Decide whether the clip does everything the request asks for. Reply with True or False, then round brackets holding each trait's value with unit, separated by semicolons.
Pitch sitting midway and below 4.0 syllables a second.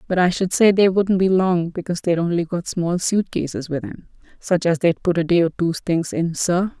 False (175 Hz; 5.2 syllables/s)